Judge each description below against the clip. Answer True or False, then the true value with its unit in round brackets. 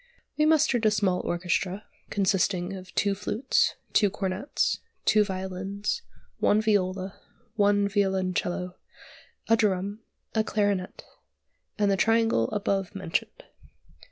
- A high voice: True (200 Hz)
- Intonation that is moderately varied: False (2.1 semitones)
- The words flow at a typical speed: False (110 wpm)